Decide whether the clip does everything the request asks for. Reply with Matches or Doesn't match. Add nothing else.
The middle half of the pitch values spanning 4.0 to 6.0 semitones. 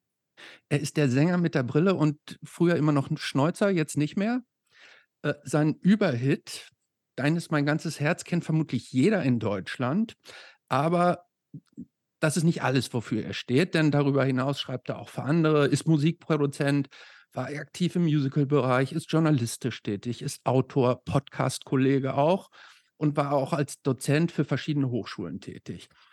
Doesn't match